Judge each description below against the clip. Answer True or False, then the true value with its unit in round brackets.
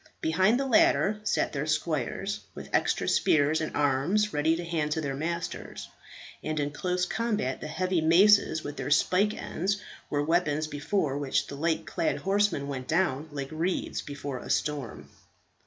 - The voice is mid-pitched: True (160 Hz)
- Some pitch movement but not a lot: True (4.3 semitones)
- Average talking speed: True (165 wpm)